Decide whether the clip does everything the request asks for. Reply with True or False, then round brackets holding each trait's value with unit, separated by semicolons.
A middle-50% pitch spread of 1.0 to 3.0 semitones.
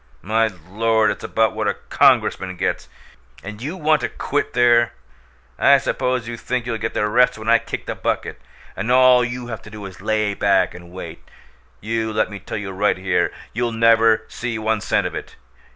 True (2.6 semitones)